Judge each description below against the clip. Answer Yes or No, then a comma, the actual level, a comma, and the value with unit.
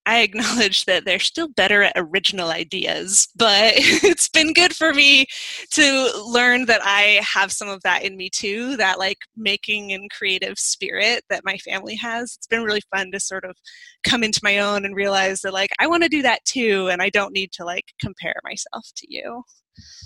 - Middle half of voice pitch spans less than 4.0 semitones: No, average, 4.6 semitones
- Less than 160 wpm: No, average, 200 wpm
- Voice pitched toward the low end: No, high, 210 Hz